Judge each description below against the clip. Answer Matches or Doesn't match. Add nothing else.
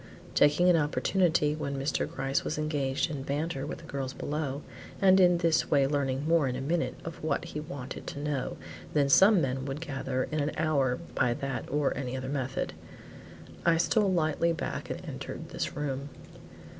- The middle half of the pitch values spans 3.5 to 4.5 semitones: Doesn't match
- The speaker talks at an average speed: Matches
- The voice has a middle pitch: Matches